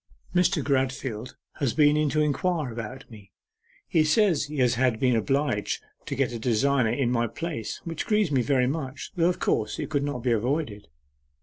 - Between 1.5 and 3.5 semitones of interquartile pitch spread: No, average, 4.4 semitones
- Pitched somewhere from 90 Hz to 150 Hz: Yes, low, 135 Hz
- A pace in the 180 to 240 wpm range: Yes, average, 185 wpm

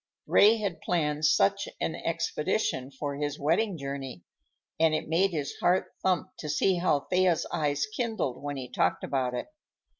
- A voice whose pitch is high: No, medium, 155 Hz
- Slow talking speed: No, average, 160 wpm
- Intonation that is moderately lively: Yes, average, 4.7 semitones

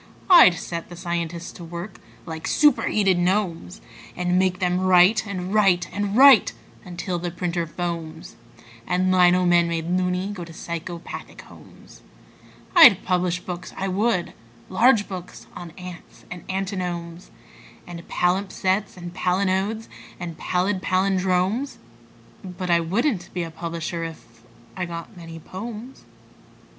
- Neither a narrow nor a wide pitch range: No, narrow, 2.0 semitones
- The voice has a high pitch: No, medium, 180 Hz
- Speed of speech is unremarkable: No, slow, 130 wpm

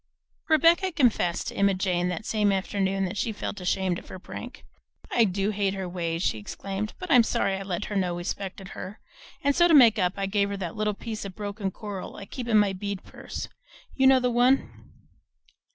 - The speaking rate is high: Yes, fast, 215 wpm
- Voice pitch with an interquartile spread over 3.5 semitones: No, average, 3.0 semitones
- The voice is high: Yes, high, 200 Hz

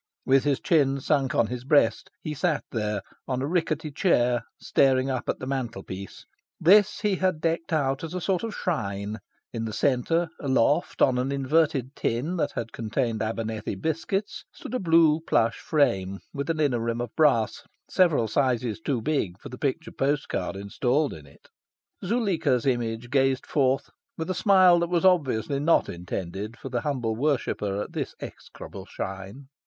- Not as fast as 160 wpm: No, average, 170 wpm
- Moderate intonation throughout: No, wide, 5.7 semitones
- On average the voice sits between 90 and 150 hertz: Yes, low, 135 Hz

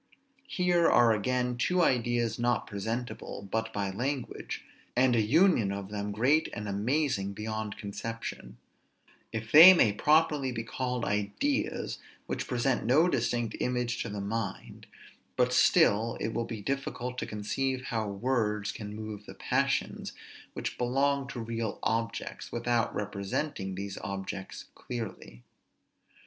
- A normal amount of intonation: Yes, average, 3.5 semitones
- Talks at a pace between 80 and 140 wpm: Yes, slow, 135 wpm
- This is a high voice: No, low, 115 Hz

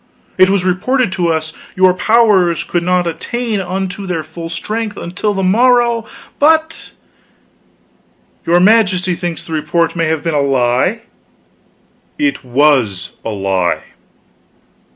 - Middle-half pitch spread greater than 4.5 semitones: Yes, average, 4.9 semitones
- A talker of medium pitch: Yes, medium, 180 Hz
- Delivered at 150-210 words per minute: No, slow, 135 wpm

